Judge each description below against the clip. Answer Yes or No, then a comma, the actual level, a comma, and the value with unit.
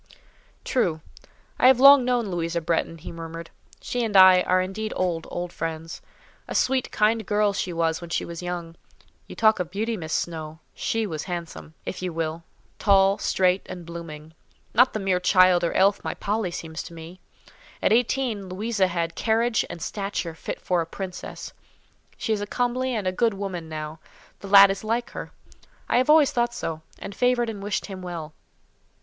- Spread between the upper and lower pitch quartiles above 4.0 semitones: Yes, average, 4.5 semitones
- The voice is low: No, medium, 185 Hz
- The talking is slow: No, average, 185 wpm